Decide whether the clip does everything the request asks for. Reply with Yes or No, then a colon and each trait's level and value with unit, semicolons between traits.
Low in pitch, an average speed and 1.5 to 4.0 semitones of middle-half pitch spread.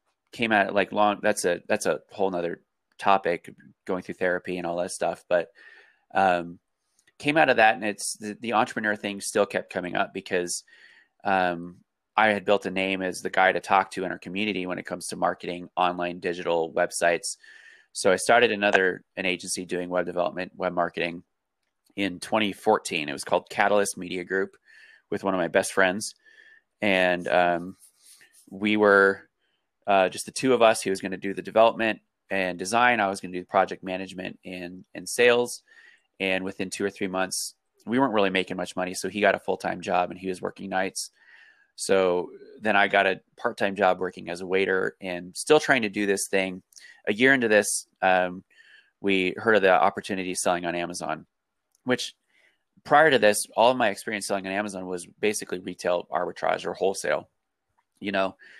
Yes: very low, 95 Hz; average, 195 wpm; narrow, 2.4 semitones